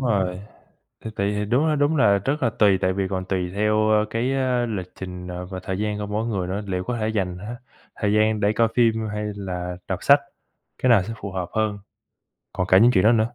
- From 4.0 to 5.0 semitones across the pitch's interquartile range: No, average, 3.4 semitones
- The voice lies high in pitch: No, low, 105 Hz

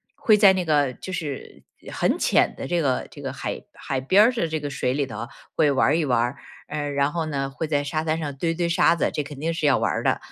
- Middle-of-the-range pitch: Yes, medium, 150 Hz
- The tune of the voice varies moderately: Yes, average, 3.2 semitones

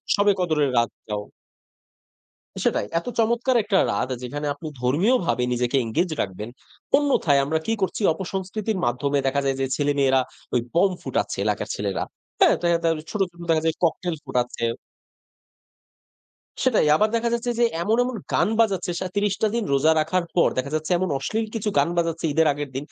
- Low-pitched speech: No, medium, 165 Hz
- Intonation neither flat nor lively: No, wide, 6.7 semitones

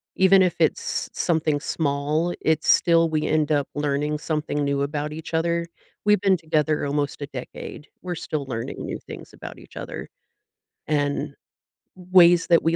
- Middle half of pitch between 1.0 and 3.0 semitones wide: Yes, narrow, 2.6 semitones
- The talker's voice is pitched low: No, medium, 155 Hz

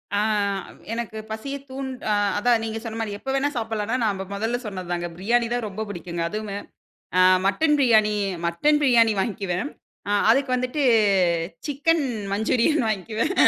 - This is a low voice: No, high, 225 Hz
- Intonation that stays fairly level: No, average, 3.9 semitones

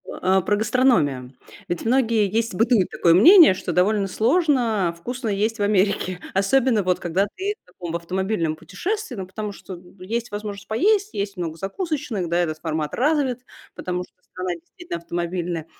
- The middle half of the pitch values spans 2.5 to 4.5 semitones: No, average, 5.2 semitones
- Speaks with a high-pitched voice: Yes, high, 200 Hz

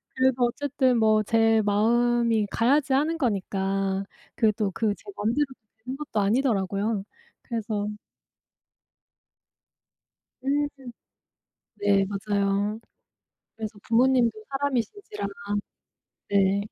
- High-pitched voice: Yes, high, 225 Hz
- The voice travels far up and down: No, average, 4.2 semitones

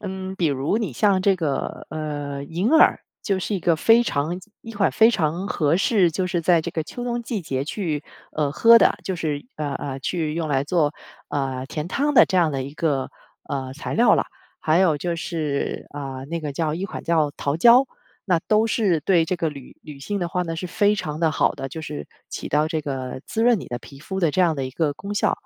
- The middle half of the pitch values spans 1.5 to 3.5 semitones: No, average, 4.7 semitones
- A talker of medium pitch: Yes, medium, 165 Hz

